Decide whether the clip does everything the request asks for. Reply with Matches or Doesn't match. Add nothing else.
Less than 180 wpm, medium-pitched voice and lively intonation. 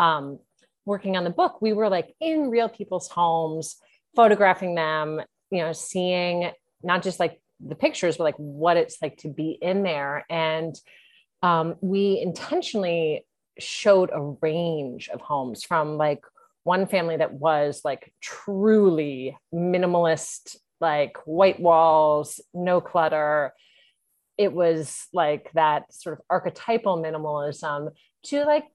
Doesn't match